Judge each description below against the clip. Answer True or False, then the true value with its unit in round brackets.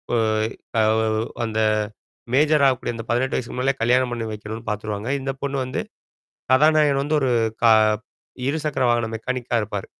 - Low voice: True (120 Hz)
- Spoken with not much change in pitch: False (3.5 semitones)